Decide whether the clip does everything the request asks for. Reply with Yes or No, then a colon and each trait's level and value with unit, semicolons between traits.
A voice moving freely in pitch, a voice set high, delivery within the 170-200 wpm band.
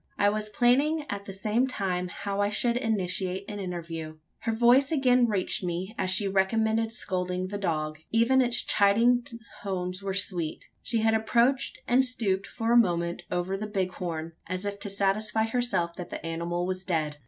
No: average, 3.9 semitones; high, 200 Hz; average, 175 wpm